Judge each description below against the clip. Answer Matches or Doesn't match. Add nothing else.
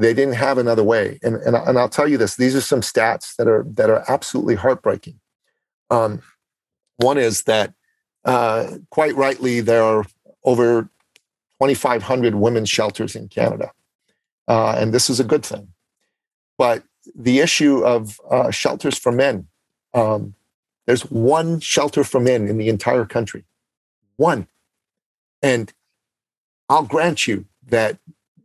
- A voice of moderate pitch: Doesn't match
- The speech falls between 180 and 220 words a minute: Doesn't match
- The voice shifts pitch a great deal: Doesn't match